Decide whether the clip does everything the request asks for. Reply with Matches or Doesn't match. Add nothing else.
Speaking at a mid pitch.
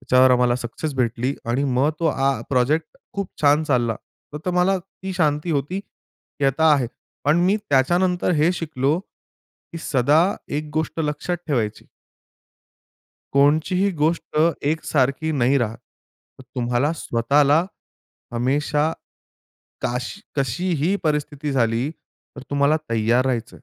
Matches